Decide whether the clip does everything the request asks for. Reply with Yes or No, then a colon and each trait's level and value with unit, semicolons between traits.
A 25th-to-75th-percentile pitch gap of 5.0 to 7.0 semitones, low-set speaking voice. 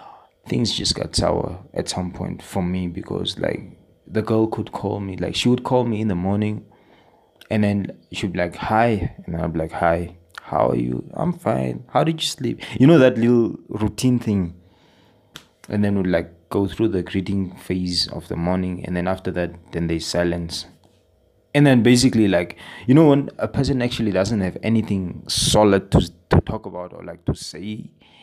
No: average, 3.9 semitones; very low, 95 Hz